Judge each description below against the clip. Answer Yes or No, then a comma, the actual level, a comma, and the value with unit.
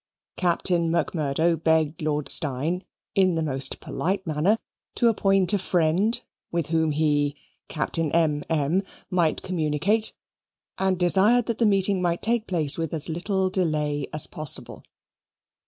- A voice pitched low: No, medium, 170 Hz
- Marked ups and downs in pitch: No, average, 3.7 semitones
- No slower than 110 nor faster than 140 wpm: Yes, slow, 135 wpm